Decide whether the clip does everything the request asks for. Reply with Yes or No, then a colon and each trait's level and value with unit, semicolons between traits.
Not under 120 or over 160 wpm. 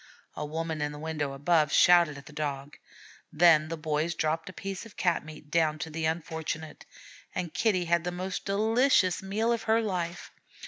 No: average, 185 wpm